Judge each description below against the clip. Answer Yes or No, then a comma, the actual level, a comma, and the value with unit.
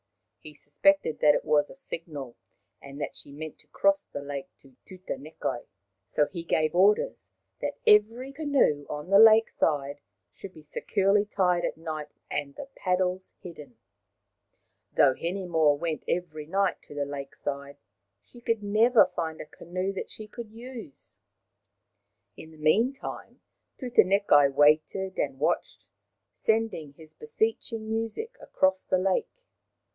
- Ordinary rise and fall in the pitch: No, wide, 6.1 semitones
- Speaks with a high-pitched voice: No, medium, 175 Hz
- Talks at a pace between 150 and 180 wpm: No, average, 140 wpm